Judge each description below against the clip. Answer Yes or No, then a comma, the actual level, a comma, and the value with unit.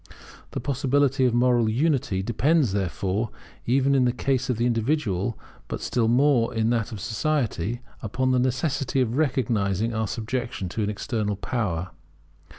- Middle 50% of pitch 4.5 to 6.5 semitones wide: No, average, 3.5 semitones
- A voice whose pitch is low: Yes, low, 120 Hz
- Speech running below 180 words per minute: Yes, average, 155 wpm